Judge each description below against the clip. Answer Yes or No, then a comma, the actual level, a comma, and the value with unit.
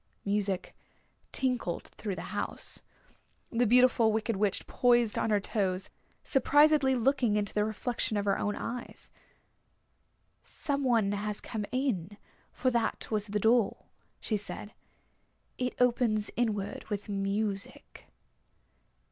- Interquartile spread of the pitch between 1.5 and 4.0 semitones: Yes, average, 3.2 semitones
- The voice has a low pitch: No, high, 215 Hz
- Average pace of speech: No, slow, 120 wpm